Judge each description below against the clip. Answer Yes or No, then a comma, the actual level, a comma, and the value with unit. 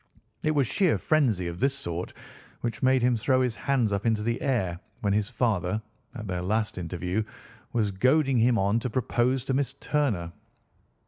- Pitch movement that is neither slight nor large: Yes, average, 4.8 semitones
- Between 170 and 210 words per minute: Yes, average, 180 wpm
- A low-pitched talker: Yes, low, 115 Hz